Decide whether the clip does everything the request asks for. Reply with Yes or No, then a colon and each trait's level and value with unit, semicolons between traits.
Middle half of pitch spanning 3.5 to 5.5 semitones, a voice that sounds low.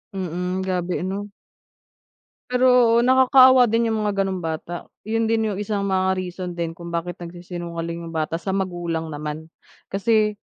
No: average, 4.2 semitones; medium, 185 Hz